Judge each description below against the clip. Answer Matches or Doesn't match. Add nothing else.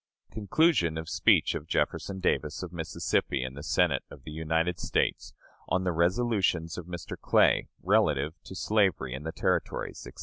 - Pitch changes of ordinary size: Matches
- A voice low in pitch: Matches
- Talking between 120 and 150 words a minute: Doesn't match